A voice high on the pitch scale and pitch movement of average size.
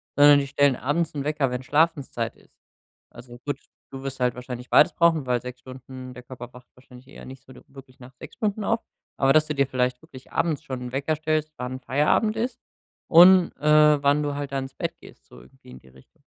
No: low, 135 Hz; average, 3.2 semitones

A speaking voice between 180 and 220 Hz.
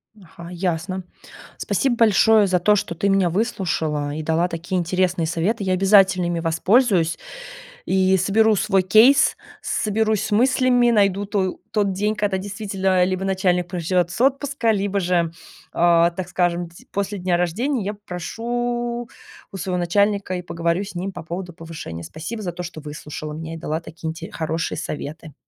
Yes: medium, 185 Hz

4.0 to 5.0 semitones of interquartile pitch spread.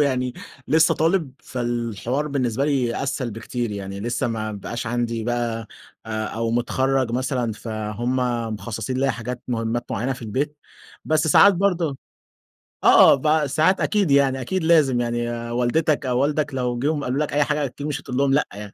No: average, 3.6 semitones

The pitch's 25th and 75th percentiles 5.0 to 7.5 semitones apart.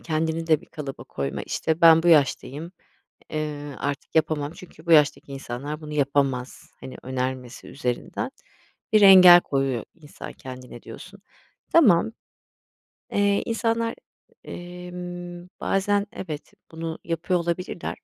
No: average, 4.0 semitones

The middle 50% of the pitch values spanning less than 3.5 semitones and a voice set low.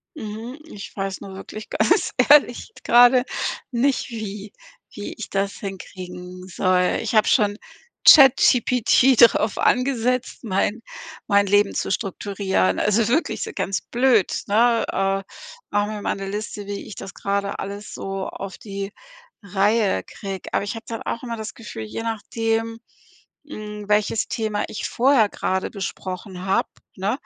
No: average, 2.8 semitones; high, 210 Hz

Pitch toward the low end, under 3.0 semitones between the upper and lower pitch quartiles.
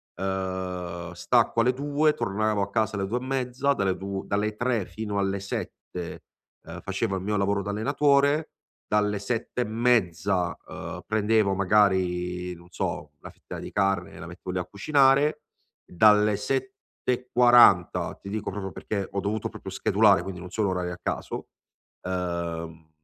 No: low, 100 Hz; average, 3.6 semitones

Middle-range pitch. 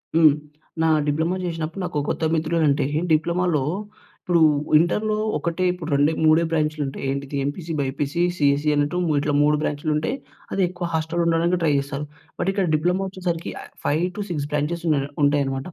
Yes: medium, 160 Hz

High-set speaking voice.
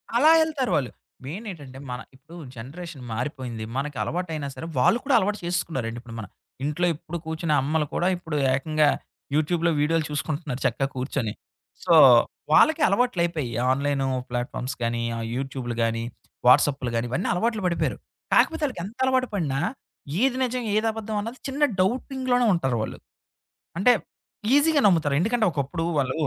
No: medium, 160 Hz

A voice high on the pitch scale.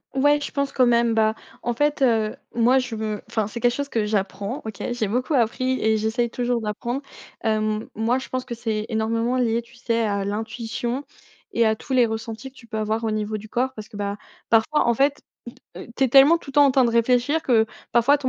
Yes: high, 235 Hz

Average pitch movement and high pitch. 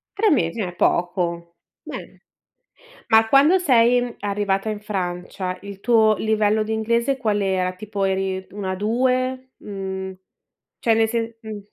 Yes: average, 3.4 semitones; high, 210 Hz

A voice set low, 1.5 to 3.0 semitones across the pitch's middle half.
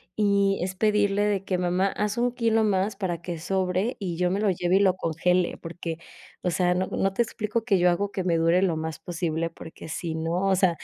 No: medium, 185 Hz; narrow, 2.5 semitones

